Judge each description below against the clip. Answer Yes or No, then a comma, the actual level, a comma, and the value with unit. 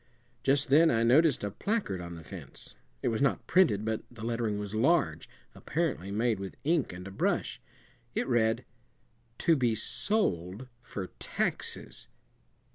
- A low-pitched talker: Yes, low, 115 Hz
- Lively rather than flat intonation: Yes, wide, 5.9 semitones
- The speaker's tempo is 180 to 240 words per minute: No, average, 150 wpm